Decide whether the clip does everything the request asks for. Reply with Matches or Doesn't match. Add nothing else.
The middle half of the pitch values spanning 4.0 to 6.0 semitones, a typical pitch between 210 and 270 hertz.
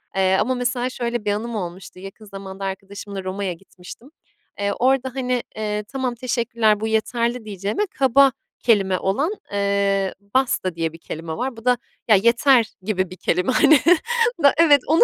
Matches